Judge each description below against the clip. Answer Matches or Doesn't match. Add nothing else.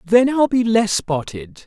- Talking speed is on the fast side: Doesn't match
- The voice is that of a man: Matches